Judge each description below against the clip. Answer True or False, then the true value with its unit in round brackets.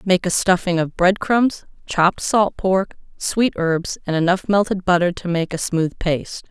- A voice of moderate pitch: True (180 Hz)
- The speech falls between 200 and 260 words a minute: False (185 wpm)